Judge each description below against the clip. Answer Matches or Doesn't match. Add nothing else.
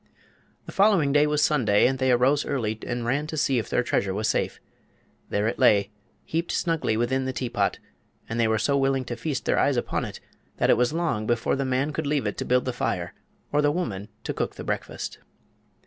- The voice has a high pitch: Doesn't match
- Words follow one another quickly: Matches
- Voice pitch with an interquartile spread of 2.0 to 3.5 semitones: Doesn't match